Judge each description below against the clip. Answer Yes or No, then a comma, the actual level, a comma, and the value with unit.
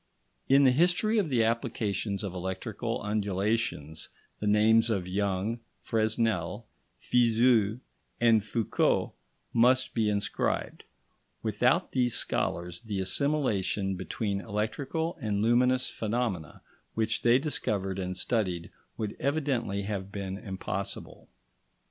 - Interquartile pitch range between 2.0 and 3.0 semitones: No, average, 3.7 semitones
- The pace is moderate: No, slow, 110 wpm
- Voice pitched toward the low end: Yes, low, 110 Hz